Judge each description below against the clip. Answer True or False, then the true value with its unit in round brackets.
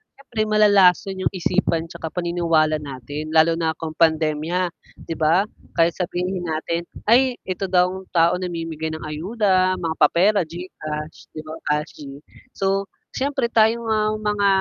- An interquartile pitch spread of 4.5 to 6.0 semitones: False (3.4 semitones)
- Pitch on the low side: False (175 Hz)